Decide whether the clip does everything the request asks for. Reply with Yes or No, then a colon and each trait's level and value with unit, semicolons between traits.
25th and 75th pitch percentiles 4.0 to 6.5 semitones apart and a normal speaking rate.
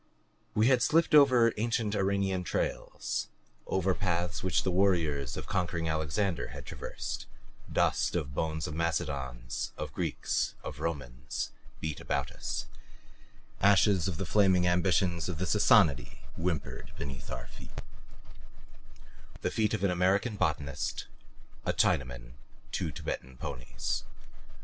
No: average, 5.2 semitones; slow, 125 wpm